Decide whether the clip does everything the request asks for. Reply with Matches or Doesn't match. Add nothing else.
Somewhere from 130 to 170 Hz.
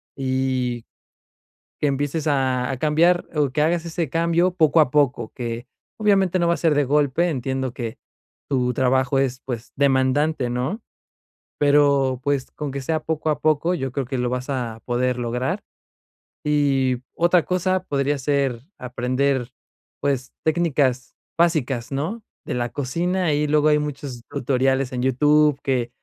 Matches